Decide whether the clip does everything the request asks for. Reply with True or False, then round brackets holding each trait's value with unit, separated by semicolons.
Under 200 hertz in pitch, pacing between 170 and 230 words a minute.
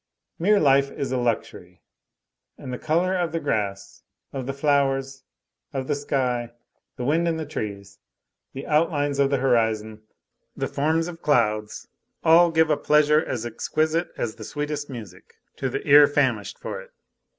False (140 Hz; 160 wpm)